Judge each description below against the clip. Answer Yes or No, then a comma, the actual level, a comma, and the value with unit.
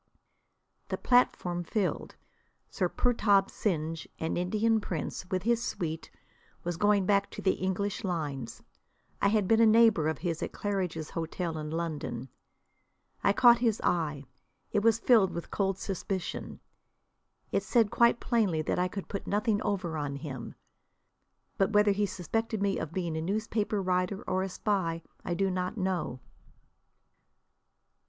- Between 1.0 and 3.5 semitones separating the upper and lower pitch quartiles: No, average, 3.9 semitones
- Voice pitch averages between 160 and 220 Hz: Yes, high, 190 Hz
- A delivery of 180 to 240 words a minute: No, average, 150 wpm